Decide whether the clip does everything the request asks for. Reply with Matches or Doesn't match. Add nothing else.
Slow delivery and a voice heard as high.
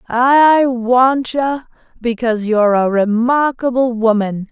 Matches